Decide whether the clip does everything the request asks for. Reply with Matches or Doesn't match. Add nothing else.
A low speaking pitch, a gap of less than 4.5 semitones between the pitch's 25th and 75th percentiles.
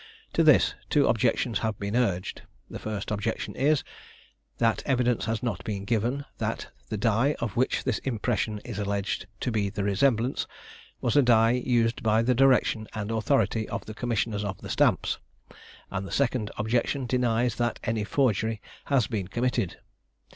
Matches